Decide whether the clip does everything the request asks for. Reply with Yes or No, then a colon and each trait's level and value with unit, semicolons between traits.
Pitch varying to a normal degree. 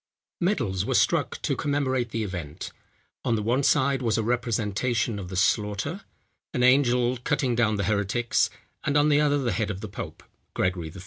Yes: average, 4.3 semitones